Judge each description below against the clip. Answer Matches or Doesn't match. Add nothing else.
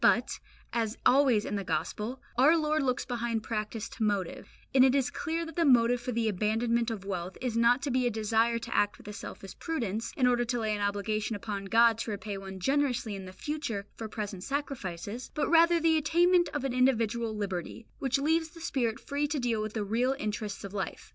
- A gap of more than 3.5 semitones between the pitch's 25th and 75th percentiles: Matches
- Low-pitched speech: Doesn't match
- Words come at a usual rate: Doesn't match